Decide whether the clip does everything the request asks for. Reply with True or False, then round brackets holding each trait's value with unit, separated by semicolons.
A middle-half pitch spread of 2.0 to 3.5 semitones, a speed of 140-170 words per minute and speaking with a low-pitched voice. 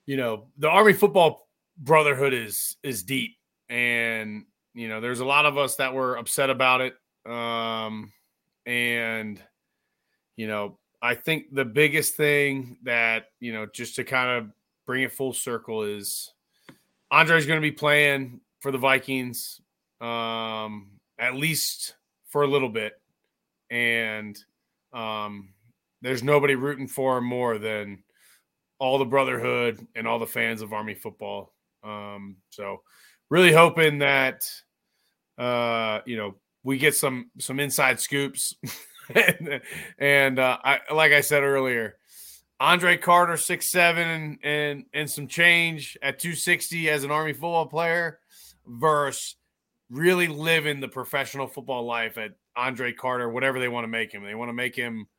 False (4.1 semitones; 150 wpm; 130 Hz)